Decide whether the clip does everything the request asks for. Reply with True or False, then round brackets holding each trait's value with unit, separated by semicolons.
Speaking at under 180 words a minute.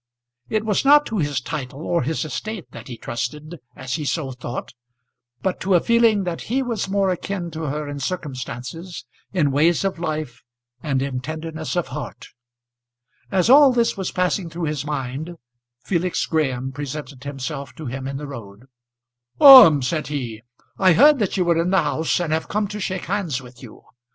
False (185 wpm)